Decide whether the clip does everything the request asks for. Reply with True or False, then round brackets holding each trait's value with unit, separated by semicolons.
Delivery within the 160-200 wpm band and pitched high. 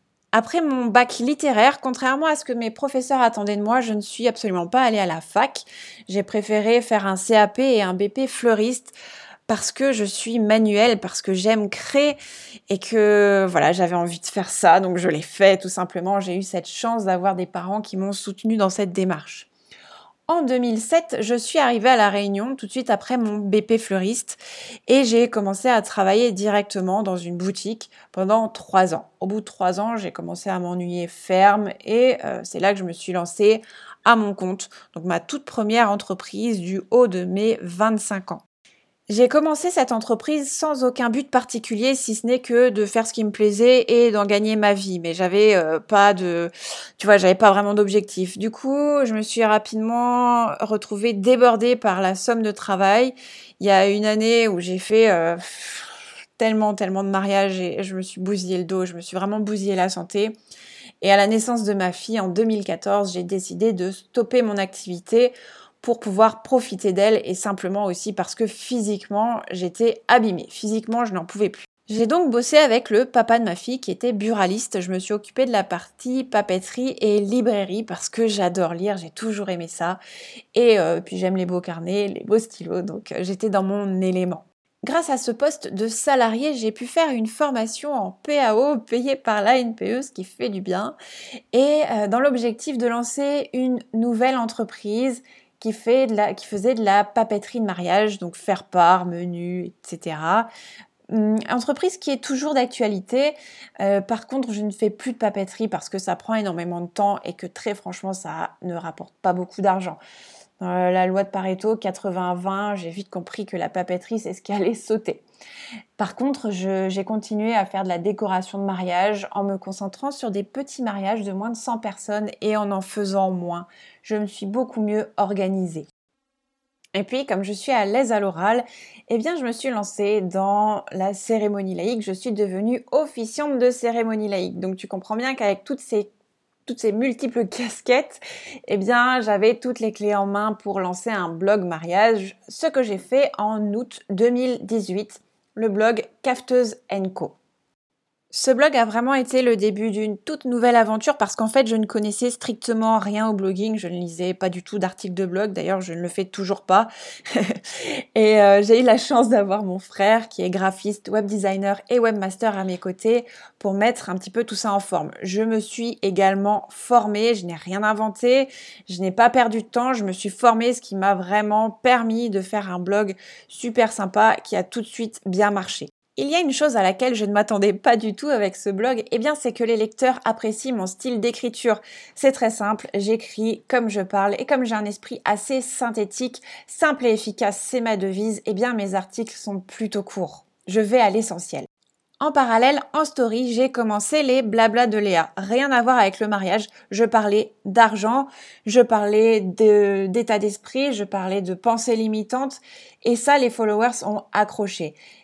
True (195 wpm; 215 Hz)